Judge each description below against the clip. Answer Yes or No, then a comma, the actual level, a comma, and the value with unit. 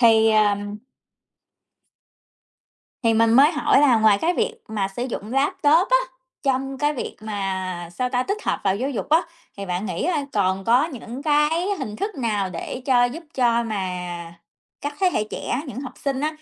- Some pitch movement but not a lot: No, wide, 5.7 semitones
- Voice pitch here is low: No, high, 245 Hz